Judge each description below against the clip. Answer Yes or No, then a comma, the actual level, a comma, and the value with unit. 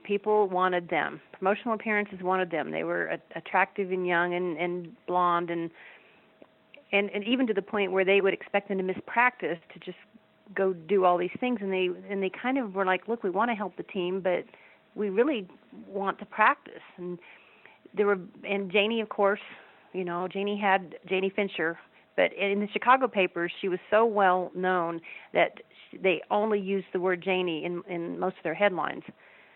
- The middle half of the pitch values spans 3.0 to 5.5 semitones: No, narrow, 2.4 semitones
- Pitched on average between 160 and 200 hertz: Yes, high, 190 Hz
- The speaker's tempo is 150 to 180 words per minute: No, average, 190 wpm